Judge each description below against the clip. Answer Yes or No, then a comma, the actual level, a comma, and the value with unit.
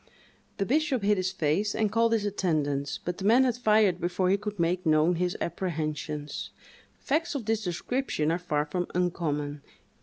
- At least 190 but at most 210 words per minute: No, average, 175 wpm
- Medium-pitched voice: Yes, medium, 180 Hz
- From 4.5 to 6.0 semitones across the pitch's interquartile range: Yes, average, 5.2 semitones